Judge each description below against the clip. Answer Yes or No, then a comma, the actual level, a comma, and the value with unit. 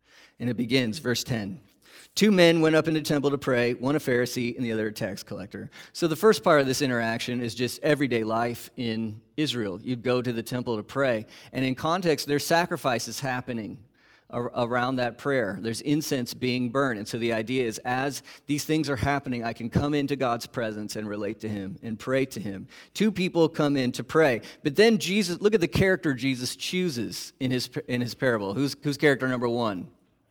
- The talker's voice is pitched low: Yes, low, 130 Hz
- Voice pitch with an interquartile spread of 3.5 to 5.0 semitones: Yes, average, 3.9 semitones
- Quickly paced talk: Yes, fast, 210 wpm